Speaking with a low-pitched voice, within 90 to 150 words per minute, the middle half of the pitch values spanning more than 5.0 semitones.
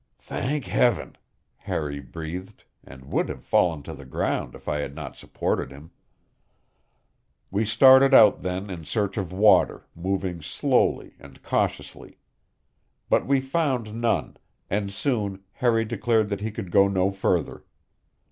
Yes: low, 100 Hz; average, 140 wpm; wide, 5.4 semitones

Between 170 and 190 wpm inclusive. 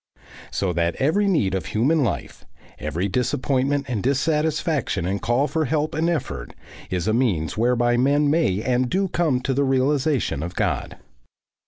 No: average, 160 wpm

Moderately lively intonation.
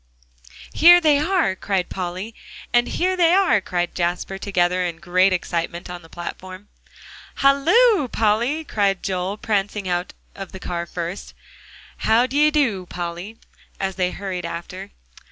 No: wide, 6.1 semitones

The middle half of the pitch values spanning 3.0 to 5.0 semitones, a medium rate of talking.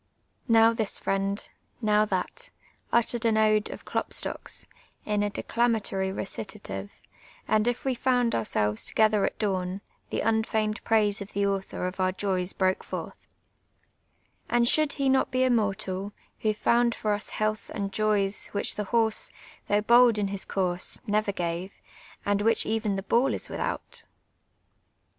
No: narrow, 2.5 semitones; average, 160 wpm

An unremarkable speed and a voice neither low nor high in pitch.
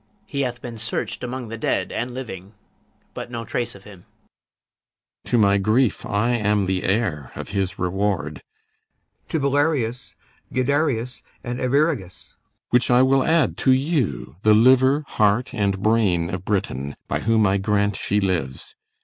No: average, 160 wpm; low, 110 Hz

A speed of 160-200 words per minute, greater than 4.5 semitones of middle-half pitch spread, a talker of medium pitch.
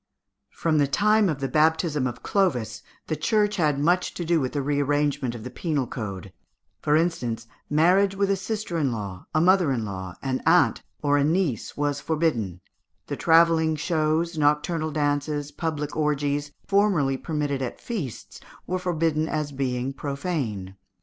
No: average, 165 wpm; average, 3.7 semitones; medium, 150 Hz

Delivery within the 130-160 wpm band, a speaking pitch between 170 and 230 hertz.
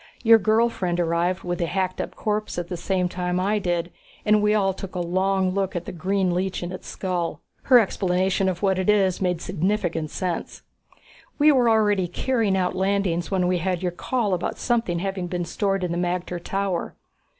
No: average, 200 wpm; medium, 185 Hz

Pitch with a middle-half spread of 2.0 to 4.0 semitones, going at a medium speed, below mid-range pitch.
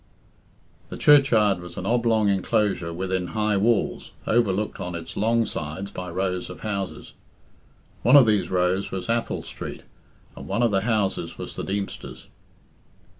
Yes: average, 3.4 semitones; average, 150 wpm; low, 100 Hz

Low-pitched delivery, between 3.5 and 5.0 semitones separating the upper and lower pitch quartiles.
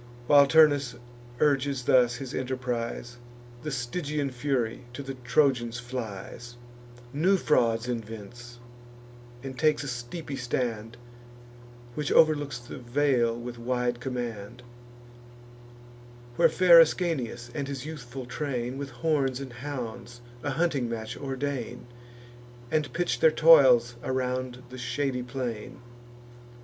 No: low, 125 Hz; average, 2.9 semitones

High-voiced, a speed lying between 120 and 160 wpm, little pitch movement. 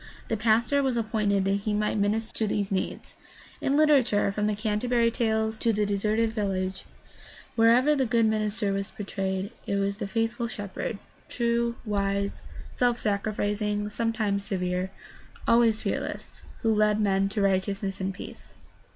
Yes: high, 210 Hz; average, 150 wpm; narrow, 2.3 semitones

